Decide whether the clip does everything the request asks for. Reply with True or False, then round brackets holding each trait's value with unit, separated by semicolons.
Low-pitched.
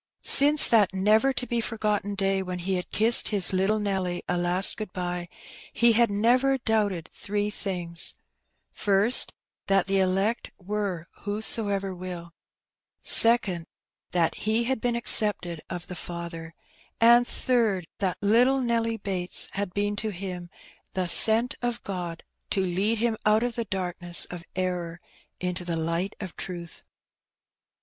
False (195 Hz)